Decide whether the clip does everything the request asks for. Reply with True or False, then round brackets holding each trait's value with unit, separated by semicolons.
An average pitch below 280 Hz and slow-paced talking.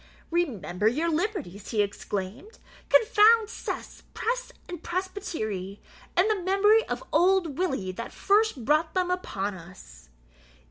False (335 Hz; 125 wpm)